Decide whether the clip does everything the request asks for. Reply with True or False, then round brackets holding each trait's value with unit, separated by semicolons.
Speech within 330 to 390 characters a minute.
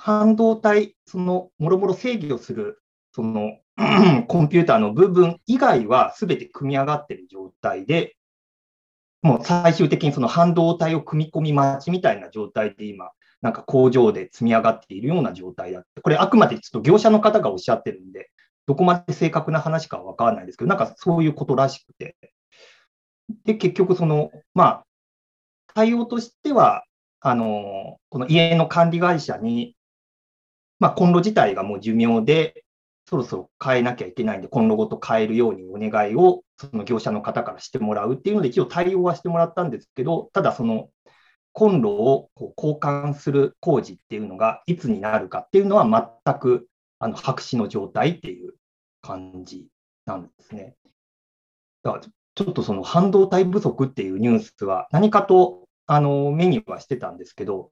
True (355 characters per minute)